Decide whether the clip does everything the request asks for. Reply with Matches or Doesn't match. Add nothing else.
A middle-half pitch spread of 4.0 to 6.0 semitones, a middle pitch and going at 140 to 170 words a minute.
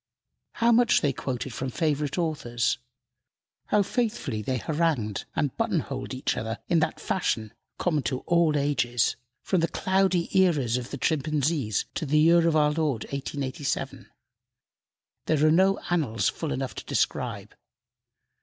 Matches